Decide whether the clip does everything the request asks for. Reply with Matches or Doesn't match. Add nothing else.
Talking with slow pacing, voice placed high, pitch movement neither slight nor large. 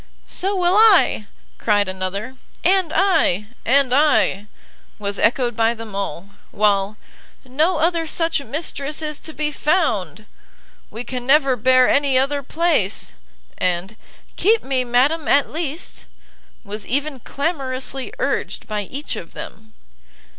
Doesn't match